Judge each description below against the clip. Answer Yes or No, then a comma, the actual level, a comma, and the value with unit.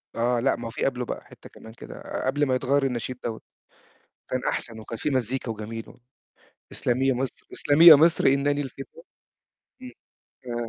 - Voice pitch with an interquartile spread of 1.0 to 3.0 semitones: Yes, average, 2.7 semitones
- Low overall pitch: Yes, low, 130 Hz